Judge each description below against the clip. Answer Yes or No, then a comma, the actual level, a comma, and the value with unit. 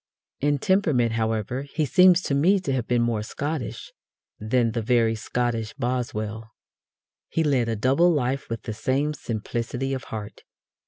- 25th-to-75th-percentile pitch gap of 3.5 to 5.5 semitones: Yes, average, 4.1 semitones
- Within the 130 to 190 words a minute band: Yes, average, 155 wpm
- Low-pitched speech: Yes, low, 125 Hz